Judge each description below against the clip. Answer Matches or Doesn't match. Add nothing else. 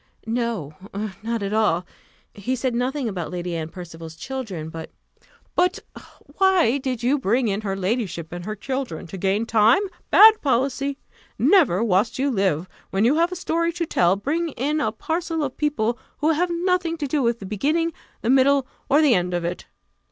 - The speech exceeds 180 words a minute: Matches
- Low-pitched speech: Doesn't match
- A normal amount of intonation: Doesn't match